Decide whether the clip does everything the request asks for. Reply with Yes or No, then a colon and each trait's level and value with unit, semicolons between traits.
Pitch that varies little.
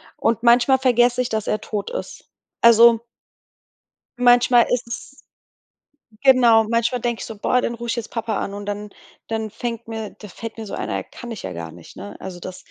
Yes: narrow, 2.1 semitones